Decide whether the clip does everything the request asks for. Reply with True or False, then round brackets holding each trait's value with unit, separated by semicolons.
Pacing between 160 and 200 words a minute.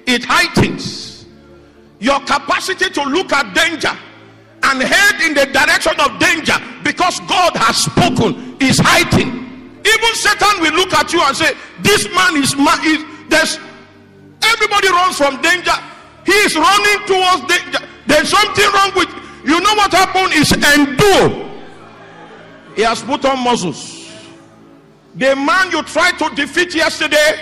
False (145 wpm)